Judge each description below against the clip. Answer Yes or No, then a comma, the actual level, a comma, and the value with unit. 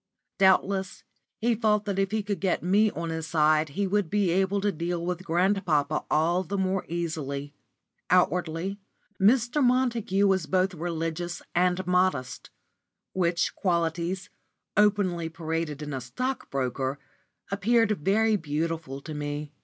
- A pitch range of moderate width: Yes, average, 3.6 semitones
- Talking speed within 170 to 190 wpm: No, slow, 135 wpm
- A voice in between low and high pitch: Yes, medium, 180 Hz